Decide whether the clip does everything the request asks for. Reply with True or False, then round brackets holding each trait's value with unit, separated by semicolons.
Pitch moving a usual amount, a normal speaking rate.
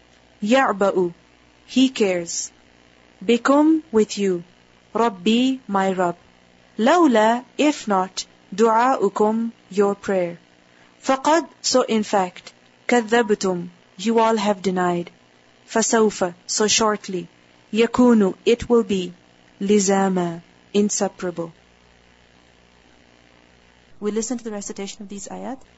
False (4.8 semitones; 95 wpm)